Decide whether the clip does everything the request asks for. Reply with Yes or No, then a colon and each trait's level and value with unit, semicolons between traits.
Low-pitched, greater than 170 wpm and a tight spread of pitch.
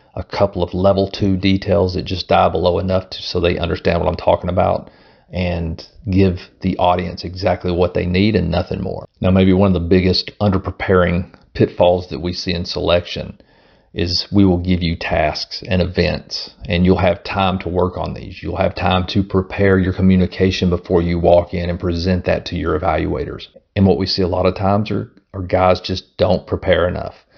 Yes: very low, 90 Hz; average, 200 wpm; narrow, 1.4 semitones